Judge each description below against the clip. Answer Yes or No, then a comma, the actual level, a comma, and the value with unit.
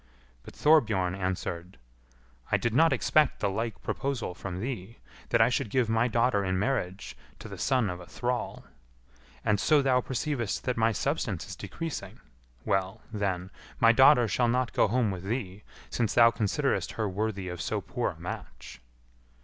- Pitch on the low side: Yes, low, 110 Hz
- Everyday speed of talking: Yes, average, 170 wpm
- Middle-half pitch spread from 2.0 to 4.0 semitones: No, average, 4.7 semitones